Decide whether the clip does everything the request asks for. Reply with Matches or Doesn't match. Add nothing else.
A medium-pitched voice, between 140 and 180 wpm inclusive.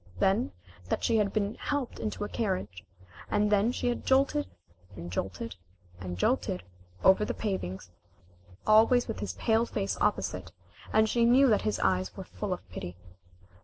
Doesn't match